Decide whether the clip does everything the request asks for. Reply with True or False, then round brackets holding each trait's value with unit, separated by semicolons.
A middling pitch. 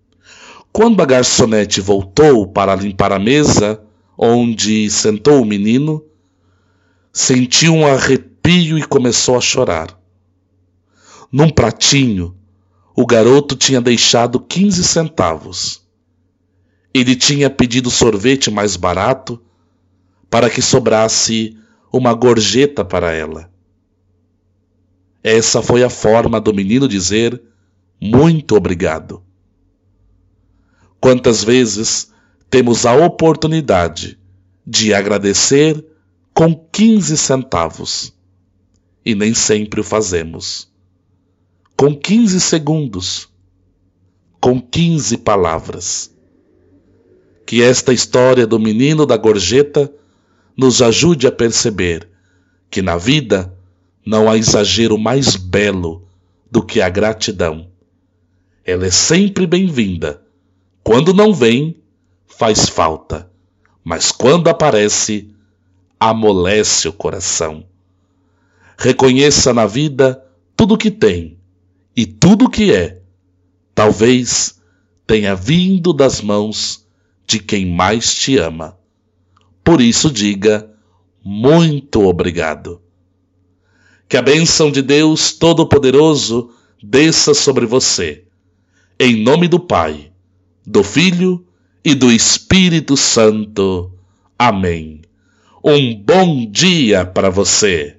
False (105 Hz)